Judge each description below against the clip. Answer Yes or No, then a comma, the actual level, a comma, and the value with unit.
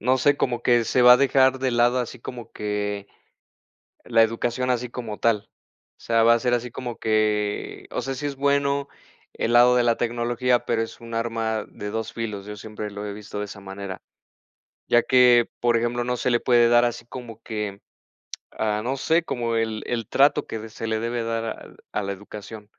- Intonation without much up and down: Yes, narrow, 2.3 semitones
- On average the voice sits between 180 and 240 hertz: No, low, 115 Hz